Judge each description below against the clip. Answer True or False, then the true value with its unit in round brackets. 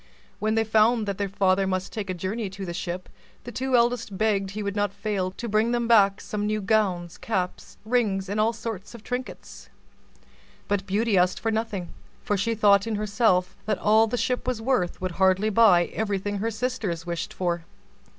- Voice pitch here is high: True (205 Hz)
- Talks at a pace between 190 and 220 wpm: True (195 wpm)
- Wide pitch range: False (2.9 semitones)